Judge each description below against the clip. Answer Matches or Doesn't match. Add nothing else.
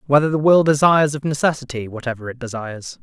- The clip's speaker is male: Matches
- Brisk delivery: Doesn't match